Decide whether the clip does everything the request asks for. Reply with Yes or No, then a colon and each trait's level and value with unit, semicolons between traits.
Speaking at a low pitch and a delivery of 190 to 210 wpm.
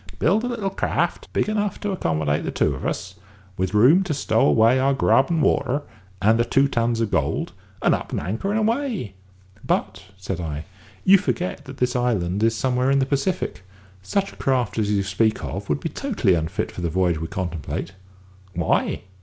Yes: low, 115 Hz; average, 195 wpm